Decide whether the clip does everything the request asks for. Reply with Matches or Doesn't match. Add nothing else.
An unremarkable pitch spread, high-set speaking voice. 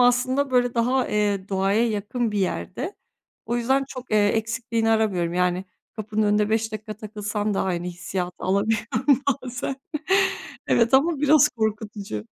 Matches